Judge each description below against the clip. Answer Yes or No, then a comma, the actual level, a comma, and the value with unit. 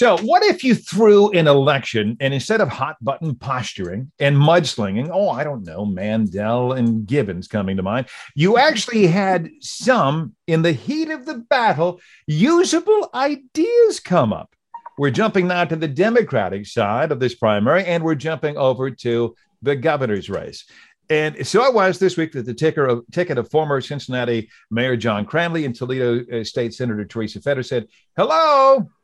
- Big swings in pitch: Yes, wide, 7.9 semitones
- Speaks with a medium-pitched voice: Yes, medium, 150 Hz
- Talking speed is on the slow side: No, average, 170 wpm